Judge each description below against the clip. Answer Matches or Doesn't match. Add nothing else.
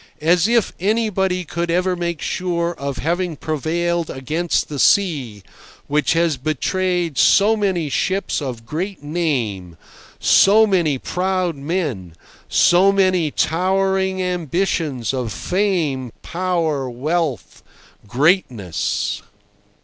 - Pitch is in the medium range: Matches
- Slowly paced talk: Matches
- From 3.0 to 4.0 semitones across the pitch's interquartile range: Doesn't match